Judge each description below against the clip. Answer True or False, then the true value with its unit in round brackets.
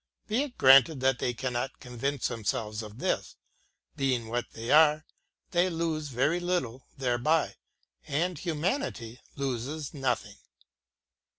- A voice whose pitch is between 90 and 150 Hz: True (135 Hz)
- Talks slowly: True (125 wpm)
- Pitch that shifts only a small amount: False (4.7 semitones)